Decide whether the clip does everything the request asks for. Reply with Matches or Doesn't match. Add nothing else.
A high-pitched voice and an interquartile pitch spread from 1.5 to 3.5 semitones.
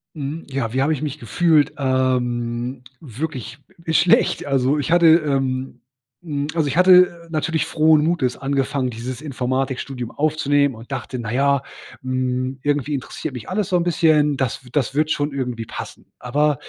Doesn't match